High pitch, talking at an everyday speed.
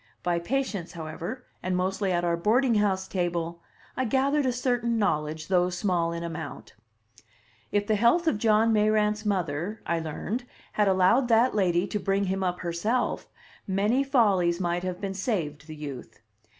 Yes: high, 195 Hz; average, 165 wpm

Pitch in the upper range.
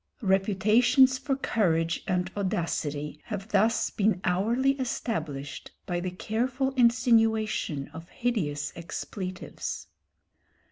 Yes: high, 200 Hz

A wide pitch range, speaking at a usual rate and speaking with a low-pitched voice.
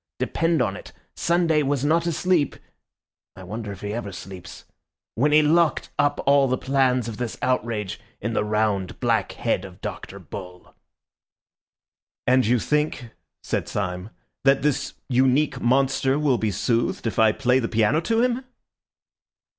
Yes: wide, 5.7 semitones; average, 155 wpm; low, 125 Hz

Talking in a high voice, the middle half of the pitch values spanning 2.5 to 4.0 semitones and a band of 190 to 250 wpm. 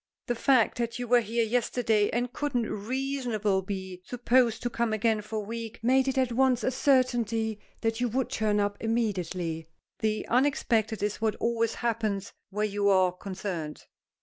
No: high, 225 Hz; average, 3.0 semitones; average, 170 wpm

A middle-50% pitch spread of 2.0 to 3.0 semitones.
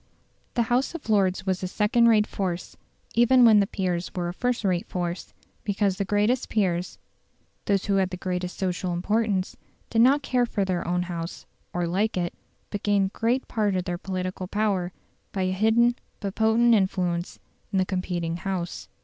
No: average, 3.4 semitones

